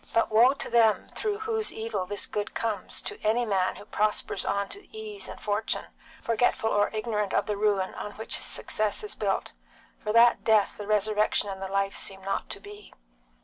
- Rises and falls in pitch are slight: Yes, narrow, 2.1 semitones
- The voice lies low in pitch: No, high, 215 Hz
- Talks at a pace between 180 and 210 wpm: Yes, average, 195 wpm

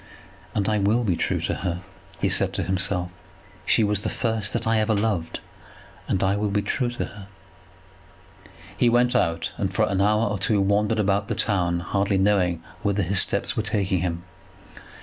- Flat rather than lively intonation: Yes, narrow, 2.2 semitones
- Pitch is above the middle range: No, low, 100 Hz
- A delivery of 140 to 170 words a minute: No, average, 190 wpm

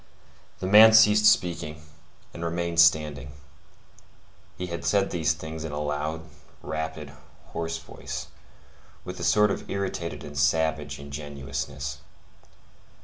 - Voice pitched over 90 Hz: No, very low, 80 Hz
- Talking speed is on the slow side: Yes, slow, 120 wpm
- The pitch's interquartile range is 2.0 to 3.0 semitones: Yes, average, 2.7 semitones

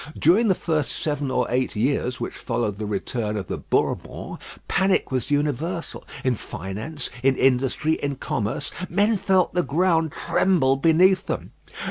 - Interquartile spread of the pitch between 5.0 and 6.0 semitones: Yes, wide, 5.5 semitones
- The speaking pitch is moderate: Yes, medium, 145 Hz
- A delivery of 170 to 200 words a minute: No, average, 150 wpm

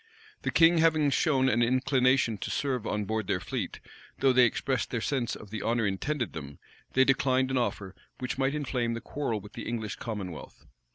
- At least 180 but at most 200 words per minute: Yes, average, 190 wpm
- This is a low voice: Yes, low, 125 Hz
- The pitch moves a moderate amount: Yes, average, 3.6 semitones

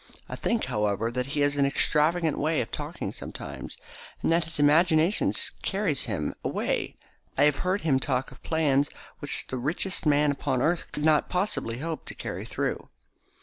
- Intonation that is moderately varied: Yes, average, 3.6 semitones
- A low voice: No, medium, 150 Hz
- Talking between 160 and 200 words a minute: Yes, average, 175 wpm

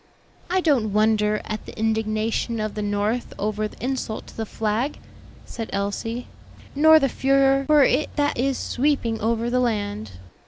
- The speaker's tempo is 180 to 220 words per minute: No, average, 160 wpm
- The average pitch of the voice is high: Yes, high, 225 Hz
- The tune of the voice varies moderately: Yes, average, 4.1 semitones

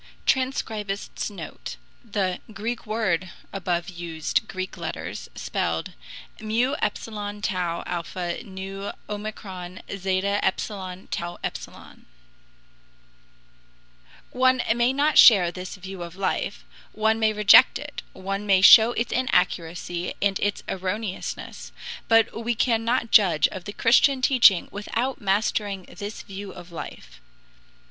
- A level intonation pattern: No, average, 3.4 semitones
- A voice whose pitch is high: Yes, high, 200 Hz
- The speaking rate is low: Yes, slow, 115 wpm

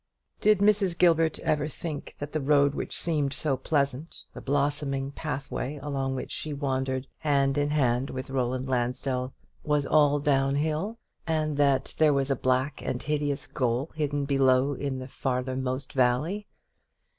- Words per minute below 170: Yes, average, 155 wpm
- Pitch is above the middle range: No, medium, 140 Hz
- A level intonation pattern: Yes, narrow, 2.2 semitones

